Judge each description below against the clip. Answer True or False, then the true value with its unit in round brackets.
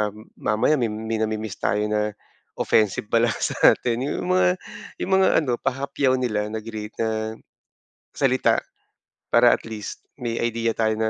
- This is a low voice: True (110 Hz)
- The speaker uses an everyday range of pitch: False (2.0 semitones)